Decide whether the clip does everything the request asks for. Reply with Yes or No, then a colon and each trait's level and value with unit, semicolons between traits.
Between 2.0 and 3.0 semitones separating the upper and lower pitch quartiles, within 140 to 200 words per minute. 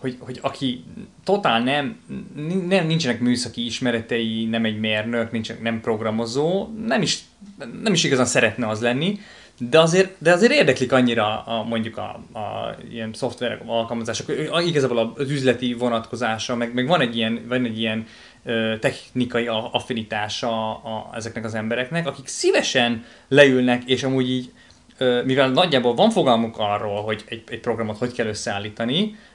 No: average, 3.4 semitones; average, 145 wpm